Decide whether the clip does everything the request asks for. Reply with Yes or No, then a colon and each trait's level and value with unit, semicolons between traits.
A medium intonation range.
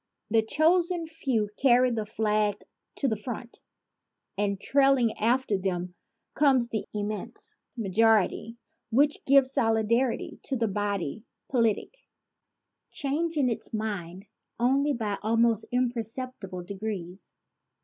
Yes: average, 4.1 semitones